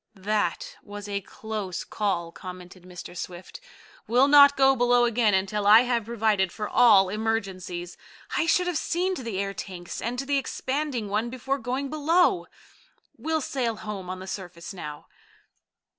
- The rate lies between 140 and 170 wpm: Yes, average, 160 wpm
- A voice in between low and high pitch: No, high, 220 Hz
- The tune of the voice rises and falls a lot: Yes, wide, 5.7 semitones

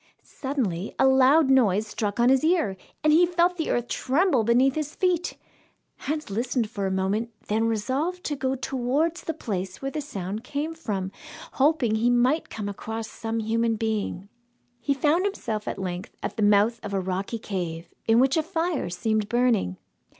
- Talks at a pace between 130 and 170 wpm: No, average, 180 wpm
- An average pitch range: No, wide, 5.9 semitones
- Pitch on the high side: Yes, high, 240 Hz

